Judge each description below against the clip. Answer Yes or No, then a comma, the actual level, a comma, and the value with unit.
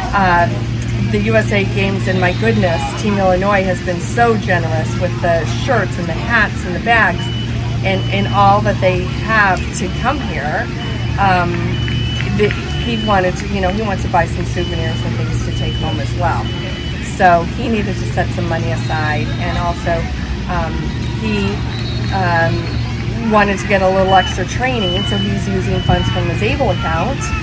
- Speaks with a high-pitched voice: No, low, 115 Hz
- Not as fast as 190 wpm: Yes, average, 175 wpm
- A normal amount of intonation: No, wide, 8.5 semitones